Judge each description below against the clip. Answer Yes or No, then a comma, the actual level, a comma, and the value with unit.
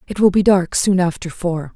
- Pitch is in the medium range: Yes, medium, 180 Hz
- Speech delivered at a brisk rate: Yes, fast, 240 wpm